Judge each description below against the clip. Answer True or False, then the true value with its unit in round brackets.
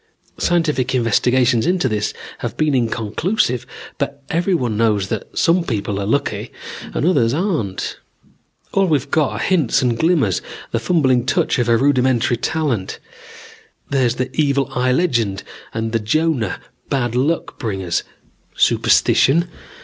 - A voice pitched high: False (130 Hz)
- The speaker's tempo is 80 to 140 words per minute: True (135 wpm)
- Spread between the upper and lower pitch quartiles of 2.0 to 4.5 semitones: False (5.3 semitones)